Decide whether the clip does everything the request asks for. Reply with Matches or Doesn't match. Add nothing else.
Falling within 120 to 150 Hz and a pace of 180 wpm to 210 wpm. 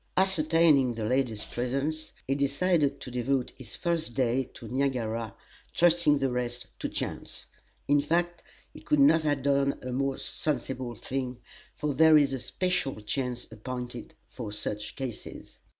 Doesn't match